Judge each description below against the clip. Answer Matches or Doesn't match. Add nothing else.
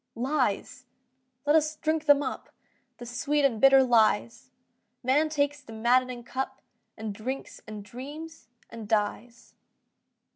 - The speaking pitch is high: Matches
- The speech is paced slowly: Matches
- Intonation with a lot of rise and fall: Doesn't match